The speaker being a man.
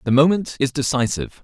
Yes: male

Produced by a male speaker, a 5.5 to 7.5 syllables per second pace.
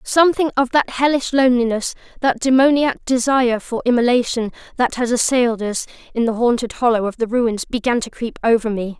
No: female; 5.7 syllables/s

